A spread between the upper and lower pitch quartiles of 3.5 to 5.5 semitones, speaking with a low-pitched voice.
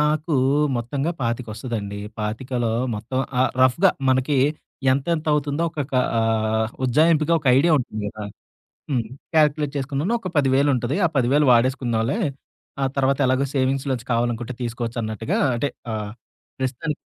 Yes: average, 3.8 semitones; low, 130 Hz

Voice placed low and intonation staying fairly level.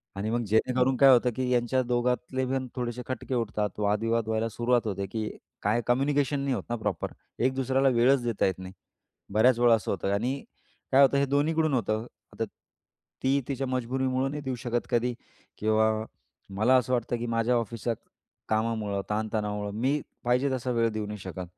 No: low, 120 Hz; average, 3.1 semitones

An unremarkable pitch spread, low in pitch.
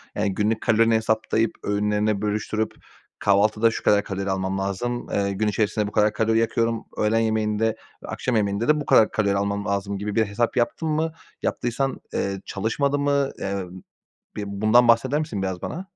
No: narrow, 2.3 semitones; low, 110 Hz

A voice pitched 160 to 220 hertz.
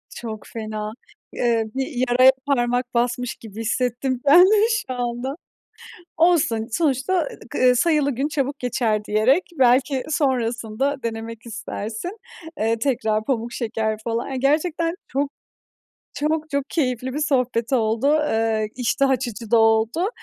No: very high, 250 Hz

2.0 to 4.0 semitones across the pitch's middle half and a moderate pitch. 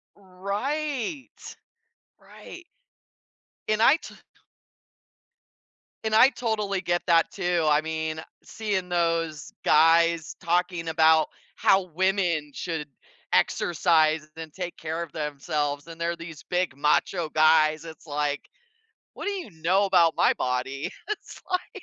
Yes: average, 3.6 semitones; medium, 170 Hz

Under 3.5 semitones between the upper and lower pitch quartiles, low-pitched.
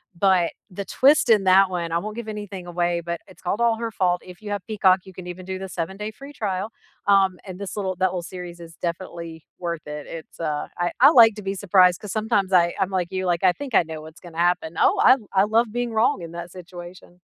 No: average, 2.9 semitones; medium, 185 Hz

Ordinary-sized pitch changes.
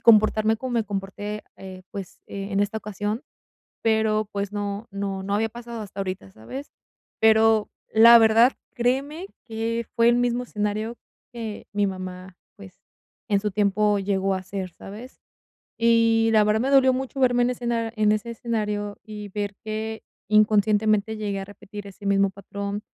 No: narrow, 2.3 semitones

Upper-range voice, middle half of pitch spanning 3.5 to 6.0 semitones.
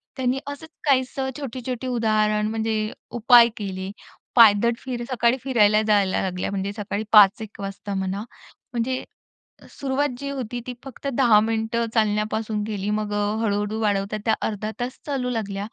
No: high, 220 Hz; average, 3.1 semitones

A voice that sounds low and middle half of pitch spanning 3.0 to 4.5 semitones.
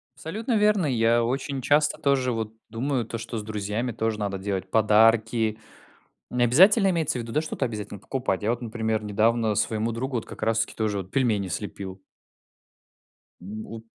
Yes: low, 115 Hz; average, 3.3 semitones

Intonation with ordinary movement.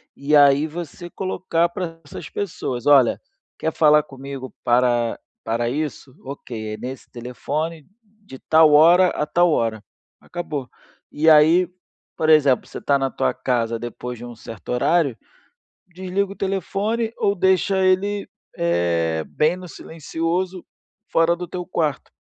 No: wide, 5.8 semitones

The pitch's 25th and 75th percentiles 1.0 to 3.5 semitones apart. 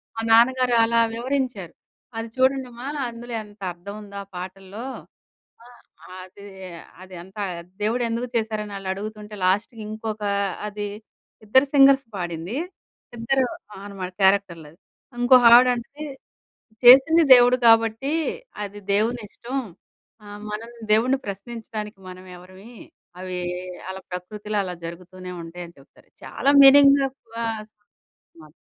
No: average, 4.2 semitones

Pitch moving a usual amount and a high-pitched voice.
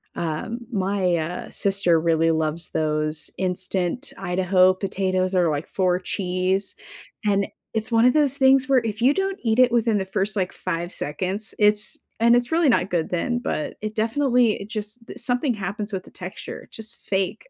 Yes: average, 4.3 semitones; high, 195 Hz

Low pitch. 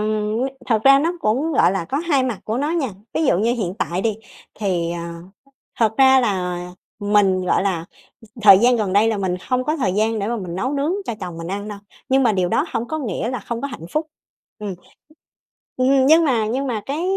No: high, 225 Hz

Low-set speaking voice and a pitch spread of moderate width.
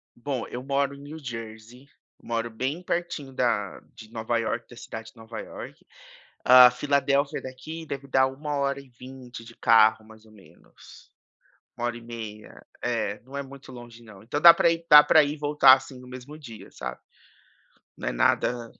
Yes: low, 125 Hz; average, 3.5 semitones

